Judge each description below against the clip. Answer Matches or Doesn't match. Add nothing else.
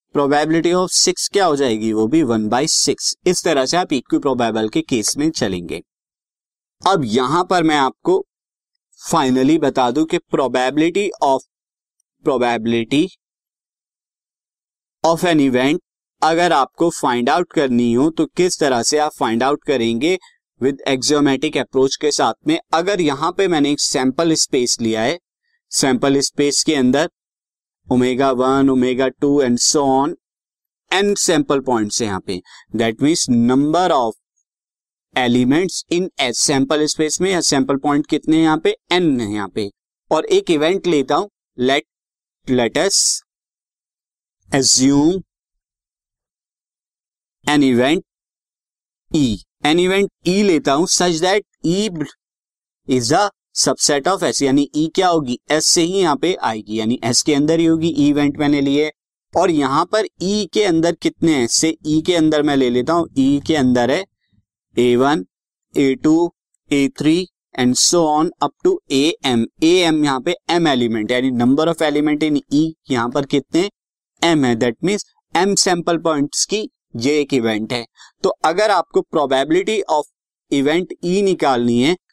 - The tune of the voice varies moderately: Matches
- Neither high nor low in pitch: Matches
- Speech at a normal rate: Matches